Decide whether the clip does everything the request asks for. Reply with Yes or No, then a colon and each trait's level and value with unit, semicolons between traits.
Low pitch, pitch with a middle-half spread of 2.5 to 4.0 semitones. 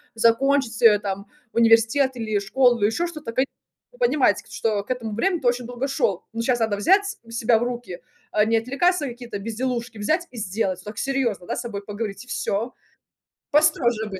No: high, 230 Hz; average, 3.6 semitones